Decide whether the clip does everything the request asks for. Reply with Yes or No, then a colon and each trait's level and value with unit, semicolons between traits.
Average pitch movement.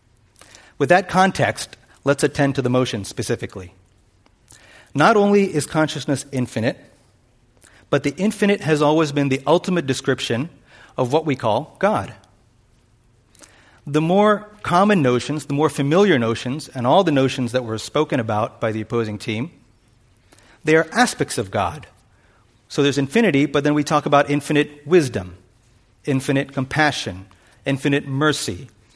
Yes: average, 4.6 semitones